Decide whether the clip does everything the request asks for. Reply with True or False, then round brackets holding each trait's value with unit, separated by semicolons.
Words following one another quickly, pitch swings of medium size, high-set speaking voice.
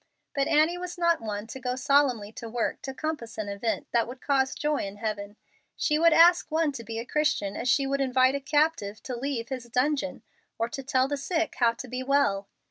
True (215 wpm; 4.1 semitones; 265 Hz)